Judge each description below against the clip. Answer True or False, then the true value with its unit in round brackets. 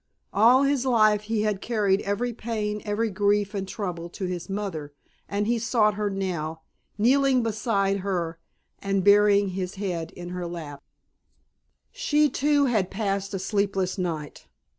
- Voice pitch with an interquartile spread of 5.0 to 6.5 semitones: False (2.8 semitones)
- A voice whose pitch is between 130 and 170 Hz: False (200 Hz)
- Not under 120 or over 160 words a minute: True (150 wpm)